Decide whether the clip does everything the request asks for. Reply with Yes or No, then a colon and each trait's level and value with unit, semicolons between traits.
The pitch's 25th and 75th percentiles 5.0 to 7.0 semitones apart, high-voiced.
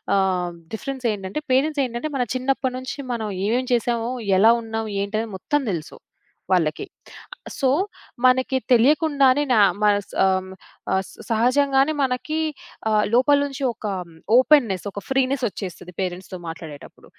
Yes: wide, 5.4 semitones; high, 240 Hz